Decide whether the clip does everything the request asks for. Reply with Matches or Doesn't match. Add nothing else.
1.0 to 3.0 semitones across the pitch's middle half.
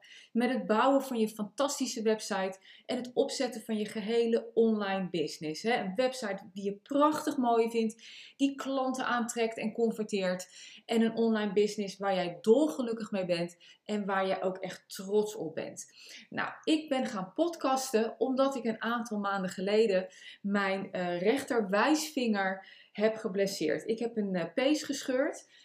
Doesn't match